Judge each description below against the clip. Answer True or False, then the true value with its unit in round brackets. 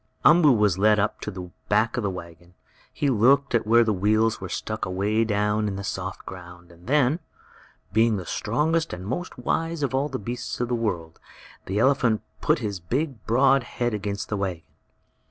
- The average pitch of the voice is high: False (110 Hz)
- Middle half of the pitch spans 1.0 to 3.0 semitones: False (4.7 semitones)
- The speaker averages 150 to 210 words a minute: True (190 wpm)